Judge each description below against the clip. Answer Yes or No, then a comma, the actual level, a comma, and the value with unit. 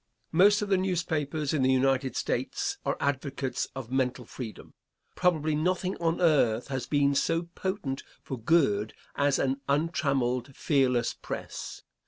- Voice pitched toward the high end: No, medium, 140 Hz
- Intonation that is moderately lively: Yes, average, 4.0 semitones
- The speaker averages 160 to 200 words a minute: No, average, 140 wpm